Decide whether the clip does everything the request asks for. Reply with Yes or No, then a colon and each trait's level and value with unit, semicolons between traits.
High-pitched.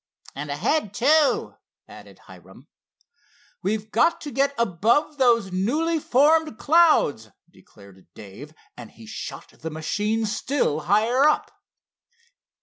Yes: high, 220 Hz